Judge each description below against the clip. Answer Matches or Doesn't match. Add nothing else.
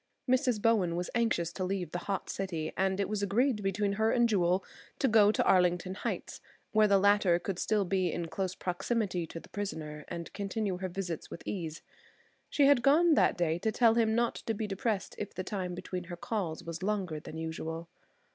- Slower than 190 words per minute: Doesn't match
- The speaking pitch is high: Matches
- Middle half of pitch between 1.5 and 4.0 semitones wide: Matches